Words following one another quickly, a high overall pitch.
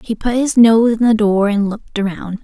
Yes: fast, 245 wpm; high, 215 Hz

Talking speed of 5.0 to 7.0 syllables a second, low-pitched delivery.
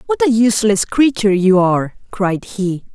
No: 5.1 syllables/s; high, 210 Hz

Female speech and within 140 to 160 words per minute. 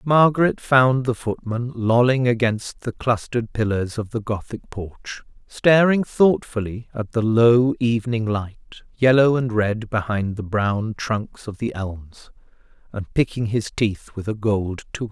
No: male; average, 150 wpm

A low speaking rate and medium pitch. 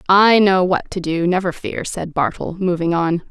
No: average, 200 wpm; medium, 180 Hz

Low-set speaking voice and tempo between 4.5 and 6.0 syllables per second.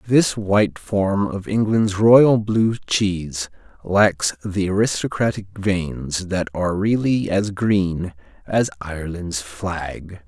No: very low, 95 Hz; 3.4 syllables/s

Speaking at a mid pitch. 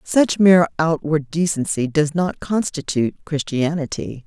Yes: medium, 160 Hz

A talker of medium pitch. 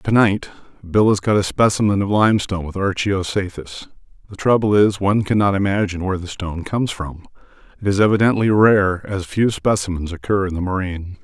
No: low, 100 Hz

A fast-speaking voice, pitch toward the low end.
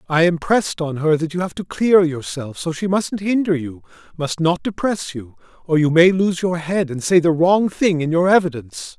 No: fast, 220 wpm; medium, 170 Hz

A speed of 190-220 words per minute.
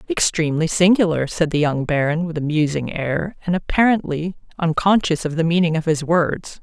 No: average, 170 wpm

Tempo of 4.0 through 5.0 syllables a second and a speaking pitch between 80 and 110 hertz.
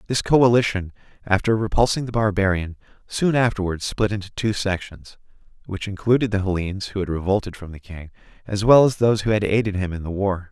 No: 6.0 syllables/s; low, 100 Hz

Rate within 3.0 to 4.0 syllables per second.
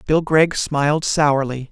Yes: 3.8 syllables/s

